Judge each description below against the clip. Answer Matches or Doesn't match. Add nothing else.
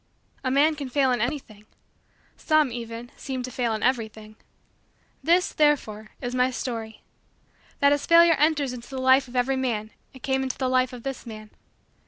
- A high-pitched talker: Matches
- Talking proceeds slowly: Doesn't match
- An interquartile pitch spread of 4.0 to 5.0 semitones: Doesn't match